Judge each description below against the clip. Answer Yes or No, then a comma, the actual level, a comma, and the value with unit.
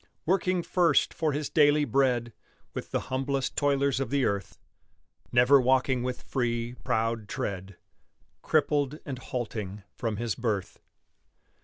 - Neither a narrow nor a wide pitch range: Yes, average, 3.5 semitones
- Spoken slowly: Yes, slow, 130 wpm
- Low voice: Yes, low, 130 Hz